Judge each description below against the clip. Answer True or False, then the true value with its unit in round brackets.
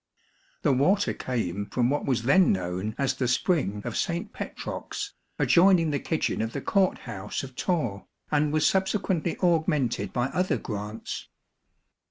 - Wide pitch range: True (7.3 semitones)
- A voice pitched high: False (140 Hz)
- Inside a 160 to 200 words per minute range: False (150 wpm)